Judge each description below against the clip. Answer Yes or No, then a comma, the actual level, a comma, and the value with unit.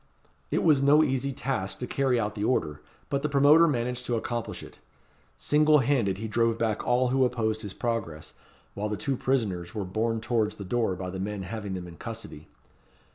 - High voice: No, low, 115 Hz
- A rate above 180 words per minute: Yes, average, 195 wpm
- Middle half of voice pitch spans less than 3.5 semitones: No, average, 4.5 semitones